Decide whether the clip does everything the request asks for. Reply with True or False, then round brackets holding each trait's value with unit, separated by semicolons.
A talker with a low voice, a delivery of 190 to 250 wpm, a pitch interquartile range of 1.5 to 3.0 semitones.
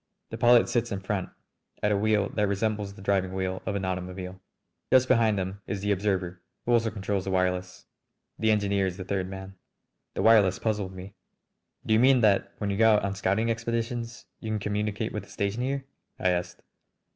True (100 Hz; 200 wpm; 2.7 semitones)